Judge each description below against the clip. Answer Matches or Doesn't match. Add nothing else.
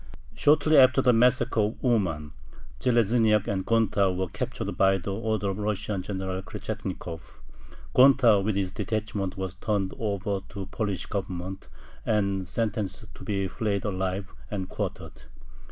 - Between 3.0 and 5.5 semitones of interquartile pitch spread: Doesn't match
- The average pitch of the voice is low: Matches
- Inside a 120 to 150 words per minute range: Matches